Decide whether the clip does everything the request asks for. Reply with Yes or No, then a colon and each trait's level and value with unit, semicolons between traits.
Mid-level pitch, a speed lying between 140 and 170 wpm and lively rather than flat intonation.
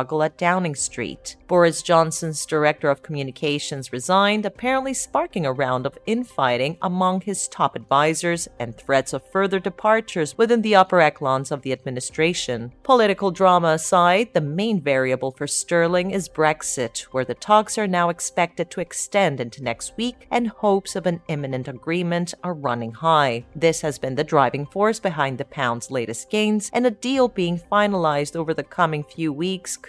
Yes: medium, 165 Hz; average, 165 wpm; wide, 5.7 semitones